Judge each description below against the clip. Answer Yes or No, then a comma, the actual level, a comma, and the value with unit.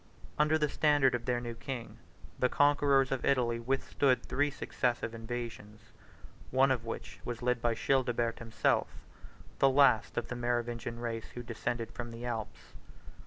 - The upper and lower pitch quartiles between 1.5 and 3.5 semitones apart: Yes, narrow, 2.4 semitones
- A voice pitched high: No, low, 120 Hz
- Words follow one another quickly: No, average, 155 wpm